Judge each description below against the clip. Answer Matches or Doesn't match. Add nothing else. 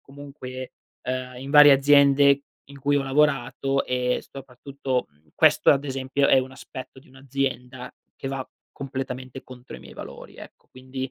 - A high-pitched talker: Doesn't match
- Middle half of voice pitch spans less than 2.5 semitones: Matches